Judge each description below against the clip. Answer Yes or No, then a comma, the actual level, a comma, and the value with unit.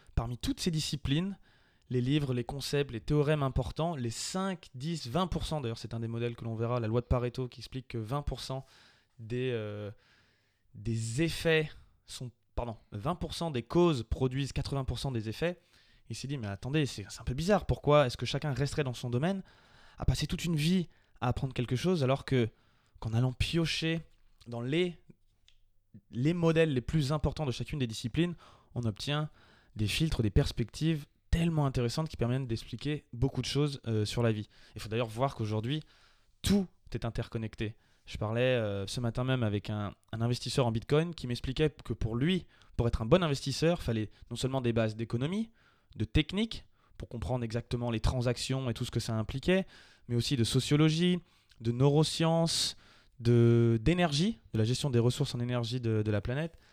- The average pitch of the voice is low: Yes, low, 125 Hz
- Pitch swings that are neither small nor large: Yes, average, 4.7 semitones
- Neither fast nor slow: Yes, average, 185 wpm